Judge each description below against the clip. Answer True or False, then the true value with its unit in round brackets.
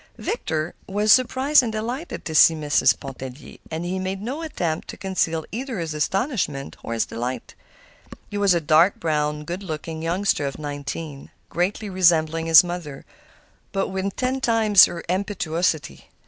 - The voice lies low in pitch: False (175 Hz)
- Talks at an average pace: True (155 wpm)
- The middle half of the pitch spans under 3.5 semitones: False (4.8 semitones)